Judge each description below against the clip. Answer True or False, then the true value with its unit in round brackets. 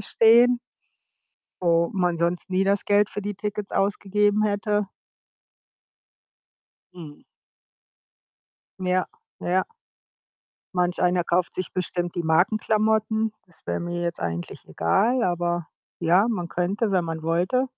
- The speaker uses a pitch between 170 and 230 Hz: True (185 Hz)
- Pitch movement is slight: False (3.2 semitones)